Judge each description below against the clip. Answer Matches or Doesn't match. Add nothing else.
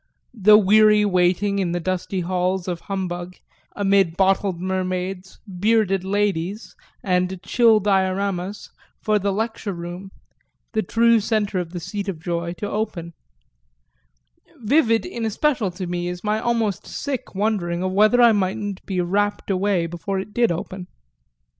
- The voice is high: Matches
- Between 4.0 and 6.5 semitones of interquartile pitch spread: Doesn't match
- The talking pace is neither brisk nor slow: Matches